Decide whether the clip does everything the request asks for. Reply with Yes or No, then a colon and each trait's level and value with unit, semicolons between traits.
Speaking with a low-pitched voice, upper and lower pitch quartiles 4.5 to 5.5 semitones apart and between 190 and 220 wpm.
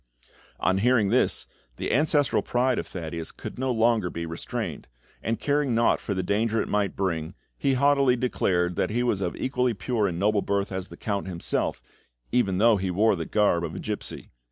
Yes: low, 105 Hz; average, 5.0 semitones; average, 200 wpm